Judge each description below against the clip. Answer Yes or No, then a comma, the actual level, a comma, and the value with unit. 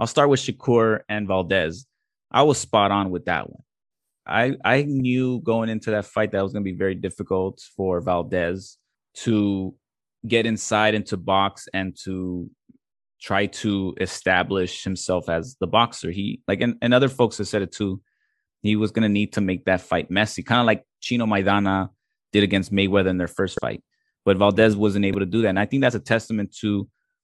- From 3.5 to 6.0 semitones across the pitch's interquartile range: No, average, 2.9 semitones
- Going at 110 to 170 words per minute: No, average, 200 wpm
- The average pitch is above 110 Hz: No, low, 100 Hz